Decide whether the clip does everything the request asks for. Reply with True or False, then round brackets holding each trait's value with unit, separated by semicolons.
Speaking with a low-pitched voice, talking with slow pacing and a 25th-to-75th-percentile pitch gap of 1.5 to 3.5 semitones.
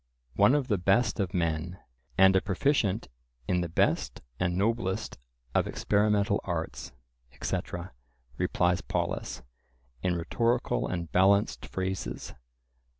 True (95 Hz; 115 wpm; 2.9 semitones)